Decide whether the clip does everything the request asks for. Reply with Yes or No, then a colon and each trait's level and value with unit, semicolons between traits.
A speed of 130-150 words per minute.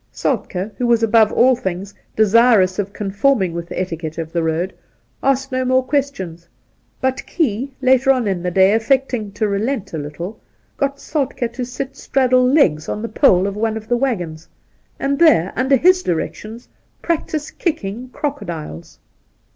No: average, 165 wpm